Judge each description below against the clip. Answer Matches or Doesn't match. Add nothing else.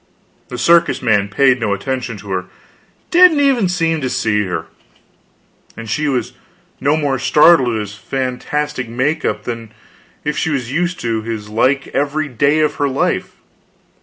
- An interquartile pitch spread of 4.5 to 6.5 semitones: Matches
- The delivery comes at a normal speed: Matches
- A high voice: Doesn't match